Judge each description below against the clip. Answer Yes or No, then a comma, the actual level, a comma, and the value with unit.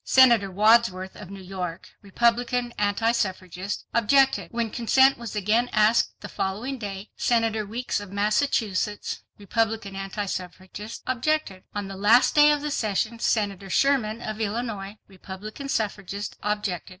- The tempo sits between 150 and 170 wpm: No, average, 140 wpm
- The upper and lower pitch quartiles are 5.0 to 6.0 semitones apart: No, average, 3.2 semitones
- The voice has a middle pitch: No, high, 215 Hz